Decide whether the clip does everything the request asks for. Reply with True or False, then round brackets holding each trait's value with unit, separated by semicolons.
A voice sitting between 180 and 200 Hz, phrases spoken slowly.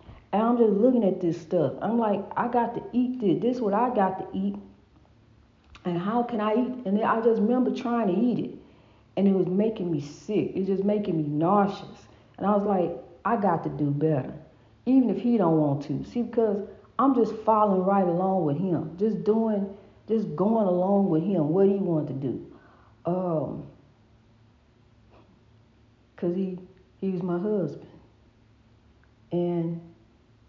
False (190 Hz; 180 wpm)